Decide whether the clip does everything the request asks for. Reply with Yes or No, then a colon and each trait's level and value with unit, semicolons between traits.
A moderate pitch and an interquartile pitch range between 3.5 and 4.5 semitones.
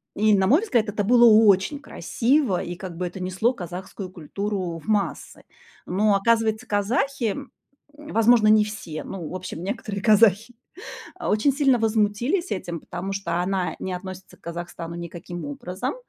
No: high, 200 Hz; average, 3.9 semitones